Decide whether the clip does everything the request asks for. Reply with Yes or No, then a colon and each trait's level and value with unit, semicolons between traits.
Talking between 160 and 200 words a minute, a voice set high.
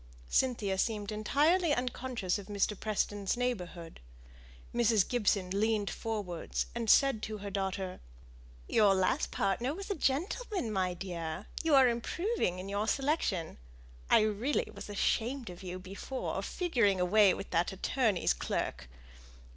No: slow, 135 wpm; high, 210 Hz